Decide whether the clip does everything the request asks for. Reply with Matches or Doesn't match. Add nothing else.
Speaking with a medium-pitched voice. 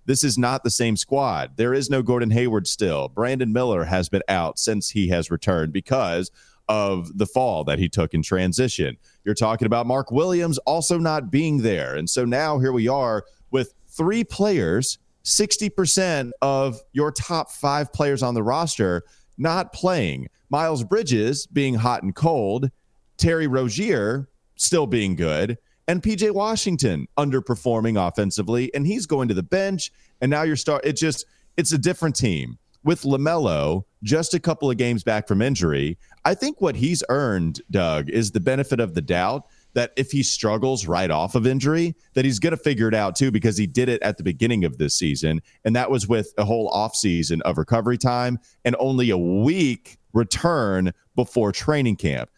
Doesn't match